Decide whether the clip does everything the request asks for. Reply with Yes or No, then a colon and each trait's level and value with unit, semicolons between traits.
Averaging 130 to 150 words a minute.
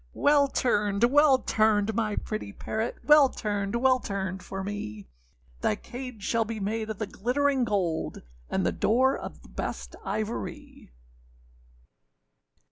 Yes: average, 140 wpm